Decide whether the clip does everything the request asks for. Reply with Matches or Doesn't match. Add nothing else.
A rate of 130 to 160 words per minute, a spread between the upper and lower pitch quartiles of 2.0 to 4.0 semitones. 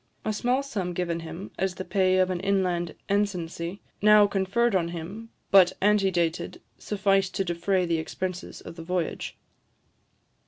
Matches